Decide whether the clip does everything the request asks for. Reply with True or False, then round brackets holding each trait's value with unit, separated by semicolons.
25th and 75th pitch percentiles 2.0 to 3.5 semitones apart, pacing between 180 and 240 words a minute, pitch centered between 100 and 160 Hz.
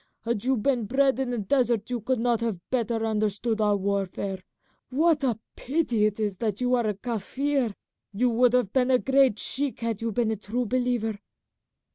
False (3.0 semitones; 190 wpm; 235 Hz)